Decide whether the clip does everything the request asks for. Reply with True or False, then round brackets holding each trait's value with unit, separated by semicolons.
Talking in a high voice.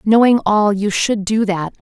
True (210 Hz)